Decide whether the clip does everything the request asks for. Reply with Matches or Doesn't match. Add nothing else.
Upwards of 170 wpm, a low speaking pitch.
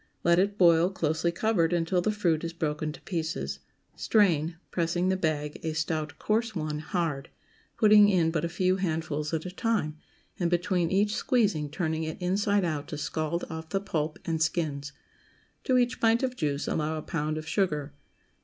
Doesn't match